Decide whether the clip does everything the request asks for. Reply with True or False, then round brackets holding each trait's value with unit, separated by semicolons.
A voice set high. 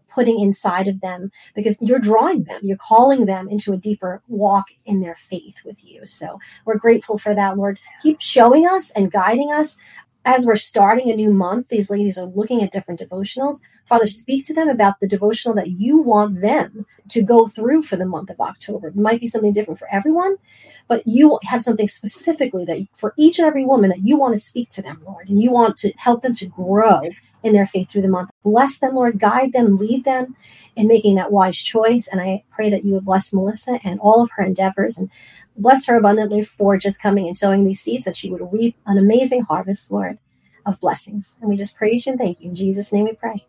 True (210 Hz)